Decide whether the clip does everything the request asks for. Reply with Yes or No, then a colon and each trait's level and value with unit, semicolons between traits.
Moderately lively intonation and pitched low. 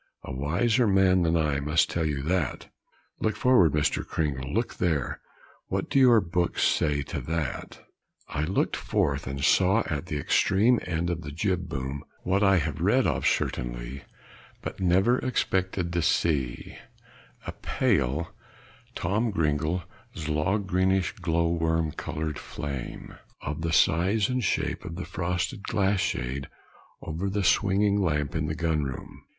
Yes: average, 4.3 semitones; very low, 85 Hz